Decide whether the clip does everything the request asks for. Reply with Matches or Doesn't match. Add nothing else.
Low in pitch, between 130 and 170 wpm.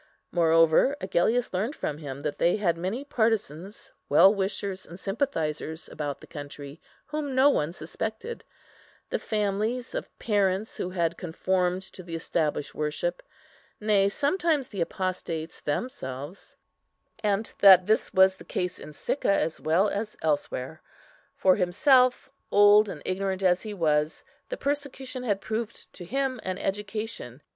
Doesn't match